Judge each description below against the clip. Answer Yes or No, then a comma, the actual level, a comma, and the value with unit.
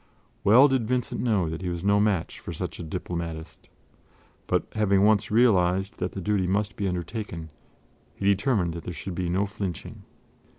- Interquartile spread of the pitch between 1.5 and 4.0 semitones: Yes, average, 3.2 semitones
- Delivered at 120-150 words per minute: No, average, 175 wpm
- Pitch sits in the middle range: No, very low, 95 Hz